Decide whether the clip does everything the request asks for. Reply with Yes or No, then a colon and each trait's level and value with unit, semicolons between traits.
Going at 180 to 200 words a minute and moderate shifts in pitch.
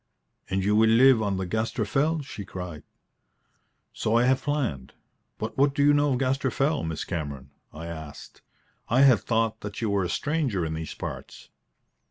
No: average, 185 wpm; wide, 7.7 semitones